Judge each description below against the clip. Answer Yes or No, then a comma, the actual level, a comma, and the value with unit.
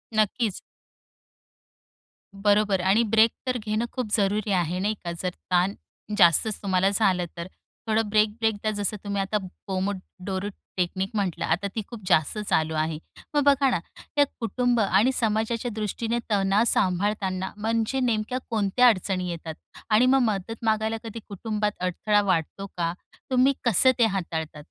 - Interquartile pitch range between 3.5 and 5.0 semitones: No, average, 3.1 semitones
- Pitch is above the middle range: Yes, high, 205 Hz